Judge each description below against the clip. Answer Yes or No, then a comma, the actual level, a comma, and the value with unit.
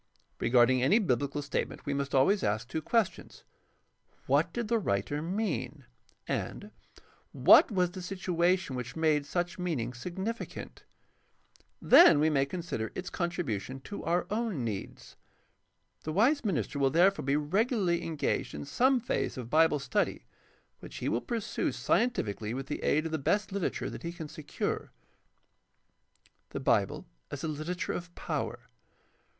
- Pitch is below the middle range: No, medium, 160 Hz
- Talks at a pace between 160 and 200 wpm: No, average, 150 wpm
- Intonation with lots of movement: Yes, wide, 5.7 semitones